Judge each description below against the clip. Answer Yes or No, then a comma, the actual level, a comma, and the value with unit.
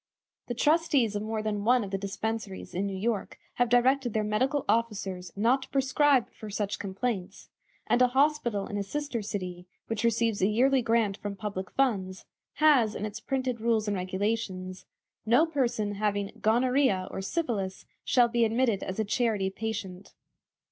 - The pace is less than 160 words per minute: No, average, 170 wpm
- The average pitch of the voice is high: Yes, high, 220 Hz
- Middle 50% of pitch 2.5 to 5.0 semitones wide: Yes, average, 3.7 semitones